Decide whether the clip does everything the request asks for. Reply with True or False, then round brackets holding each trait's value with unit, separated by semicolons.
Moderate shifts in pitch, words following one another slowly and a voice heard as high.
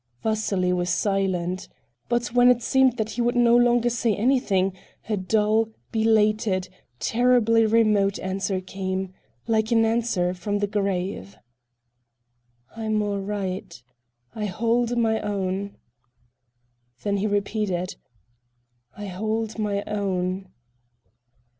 True (3.0 semitones; 110 wpm; 210 Hz)